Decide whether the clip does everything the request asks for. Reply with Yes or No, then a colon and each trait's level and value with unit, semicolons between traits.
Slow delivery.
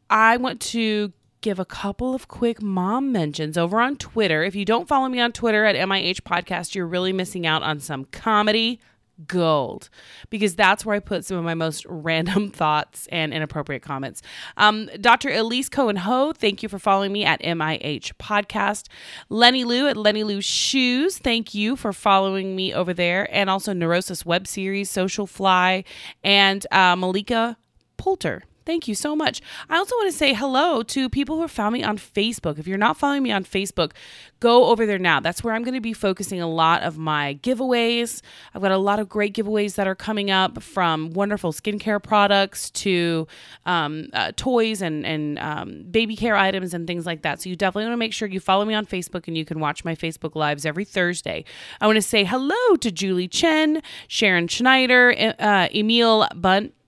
No: average, 195 wpm